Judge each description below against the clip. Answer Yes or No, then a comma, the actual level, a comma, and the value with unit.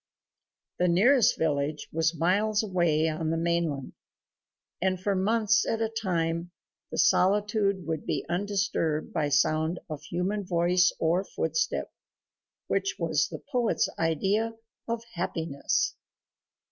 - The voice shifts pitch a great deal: No, average, 4.1 semitones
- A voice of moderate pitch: Yes, medium, 175 Hz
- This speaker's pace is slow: Yes, slow, 120 wpm